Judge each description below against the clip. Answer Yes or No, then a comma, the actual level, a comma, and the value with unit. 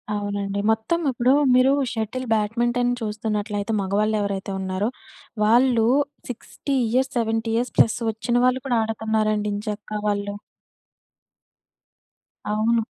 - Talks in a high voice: Yes, high, 220 Hz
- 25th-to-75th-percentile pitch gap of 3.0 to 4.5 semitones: No, narrow, 2.5 semitones